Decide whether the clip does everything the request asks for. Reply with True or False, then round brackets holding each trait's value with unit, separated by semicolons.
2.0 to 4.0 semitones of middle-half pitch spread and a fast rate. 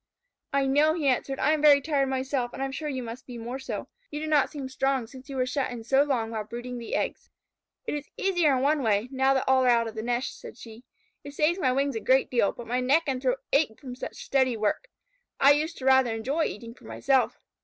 True (2.7 semitones; 255 wpm)